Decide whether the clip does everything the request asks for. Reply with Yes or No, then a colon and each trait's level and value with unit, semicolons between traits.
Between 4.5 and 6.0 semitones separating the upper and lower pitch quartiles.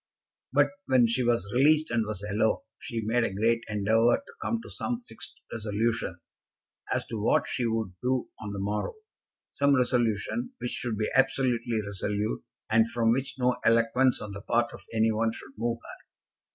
No: average, 2.7 semitones